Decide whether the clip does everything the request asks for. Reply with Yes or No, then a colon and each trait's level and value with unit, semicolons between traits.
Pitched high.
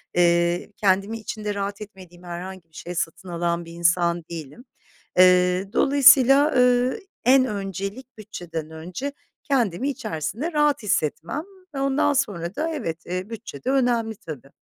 Yes: high, 195 Hz